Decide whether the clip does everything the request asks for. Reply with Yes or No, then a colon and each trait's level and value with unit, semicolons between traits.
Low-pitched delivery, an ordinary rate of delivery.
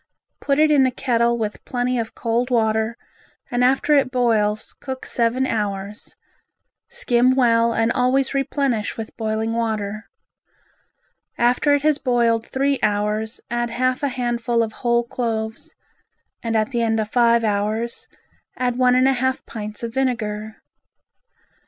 No: high, 235 Hz; average, 145 wpm